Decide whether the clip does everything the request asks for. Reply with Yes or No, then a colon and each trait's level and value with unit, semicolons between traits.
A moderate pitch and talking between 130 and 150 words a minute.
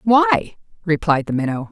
Yes: medium, 180 Hz; average, 140 wpm